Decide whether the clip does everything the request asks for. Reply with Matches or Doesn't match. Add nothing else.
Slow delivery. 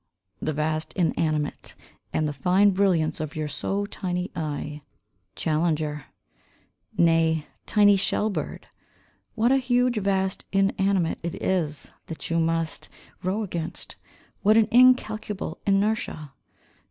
Matches